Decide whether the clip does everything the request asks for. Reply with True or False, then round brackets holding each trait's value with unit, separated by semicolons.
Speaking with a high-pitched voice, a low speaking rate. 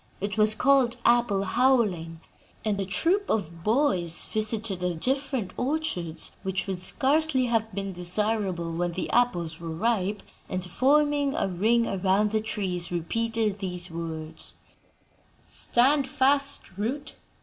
True (210 Hz; 130 wpm)